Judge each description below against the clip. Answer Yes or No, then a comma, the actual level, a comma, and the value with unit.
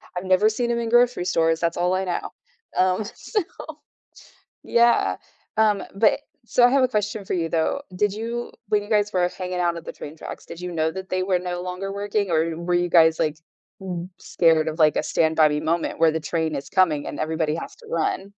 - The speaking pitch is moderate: Yes, medium, 180 Hz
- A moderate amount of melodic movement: Yes, average, 4.2 semitones